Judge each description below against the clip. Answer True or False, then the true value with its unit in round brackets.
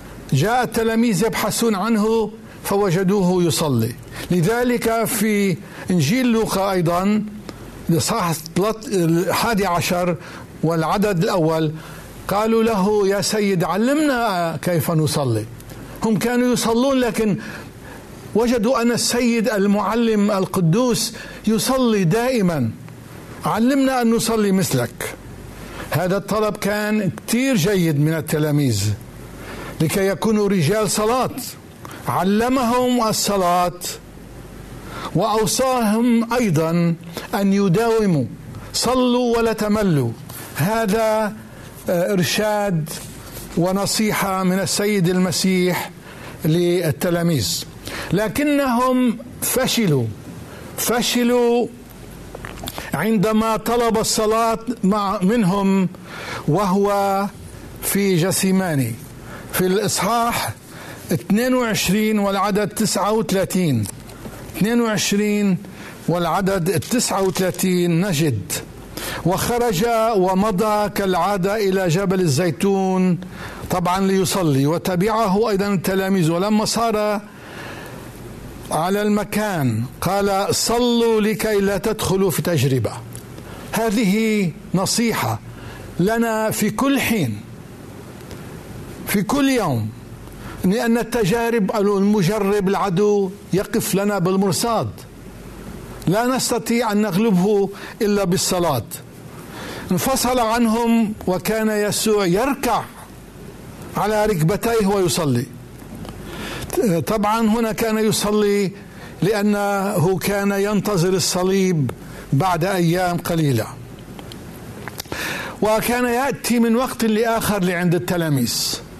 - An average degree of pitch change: True (4.3 semitones)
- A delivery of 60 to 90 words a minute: True (75 wpm)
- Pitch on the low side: False (200 Hz)